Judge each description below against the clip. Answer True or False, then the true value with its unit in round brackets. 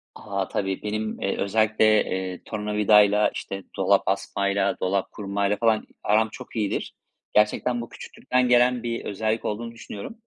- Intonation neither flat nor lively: False (2.1 semitones)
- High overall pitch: False (105 Hz)